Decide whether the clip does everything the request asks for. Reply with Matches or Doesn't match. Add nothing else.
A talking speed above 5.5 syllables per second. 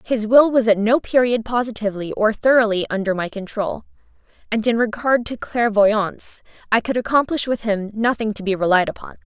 Doesn't match